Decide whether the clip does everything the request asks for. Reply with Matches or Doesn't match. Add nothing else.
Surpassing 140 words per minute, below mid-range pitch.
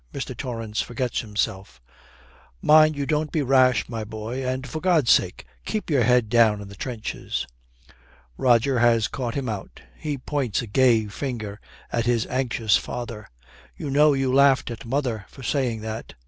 Matches